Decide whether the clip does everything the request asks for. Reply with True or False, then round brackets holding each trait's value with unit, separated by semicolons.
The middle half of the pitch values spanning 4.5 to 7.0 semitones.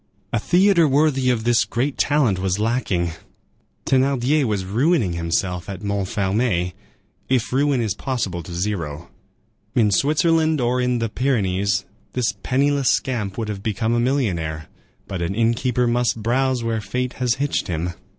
True (5.2 semitones)